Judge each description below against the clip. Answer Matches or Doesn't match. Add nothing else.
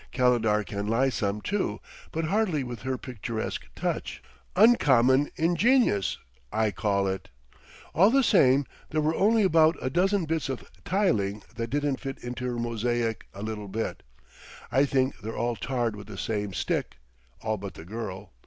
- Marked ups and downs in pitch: Matches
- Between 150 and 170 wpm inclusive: Matches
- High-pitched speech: Doesn't match